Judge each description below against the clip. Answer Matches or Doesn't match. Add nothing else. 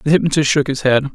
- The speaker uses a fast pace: Matches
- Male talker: Matches